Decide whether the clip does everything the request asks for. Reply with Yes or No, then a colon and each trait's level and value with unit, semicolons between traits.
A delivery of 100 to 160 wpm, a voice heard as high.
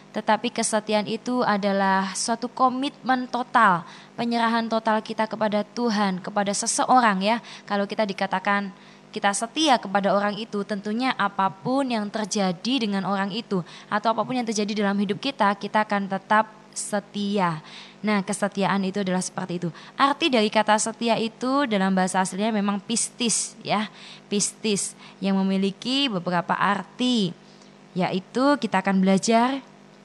Yes: average, 135 wpm; high, 210 Hz